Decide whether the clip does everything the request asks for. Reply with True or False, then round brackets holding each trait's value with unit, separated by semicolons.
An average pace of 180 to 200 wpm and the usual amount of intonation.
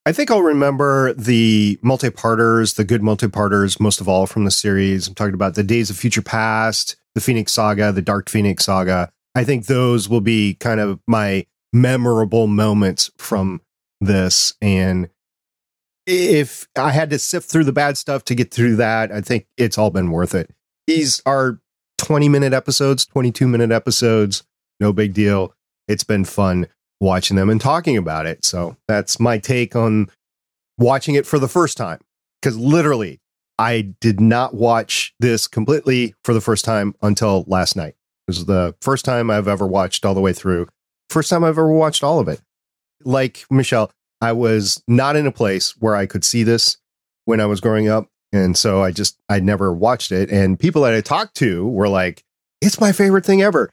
True (185 wpm; 4.4 semitones)